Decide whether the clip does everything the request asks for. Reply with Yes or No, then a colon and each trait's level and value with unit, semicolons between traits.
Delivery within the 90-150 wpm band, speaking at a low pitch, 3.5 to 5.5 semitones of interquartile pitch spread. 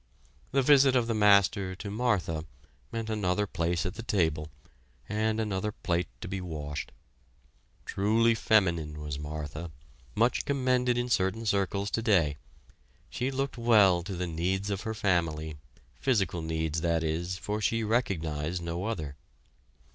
Yes: average, 140 wpm; very low, 95 Hz; average, 5.1 semitones